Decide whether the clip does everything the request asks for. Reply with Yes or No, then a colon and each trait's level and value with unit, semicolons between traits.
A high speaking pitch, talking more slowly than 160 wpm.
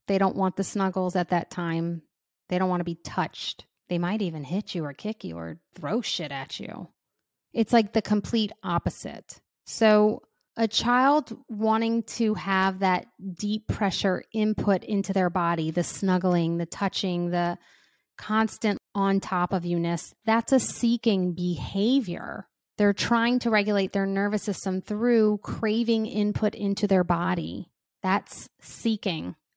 Yes: high, 195 Hz; average, 150 wpm